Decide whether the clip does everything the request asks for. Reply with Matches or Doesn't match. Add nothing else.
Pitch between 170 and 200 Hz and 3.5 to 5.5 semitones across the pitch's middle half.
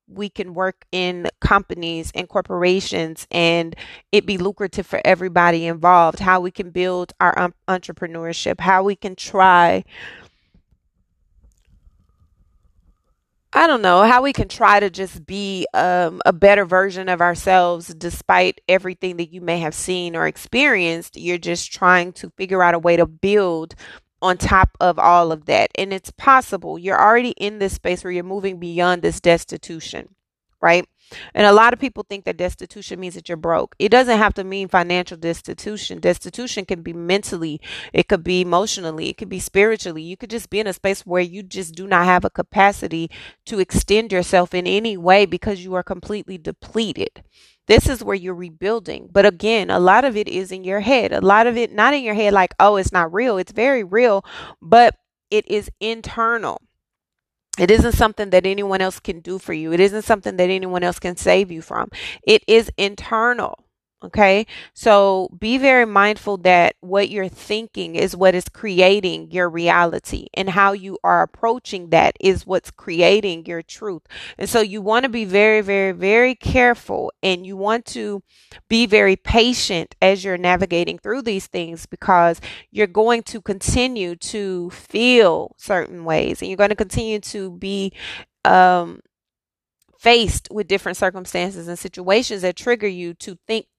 Doesn't match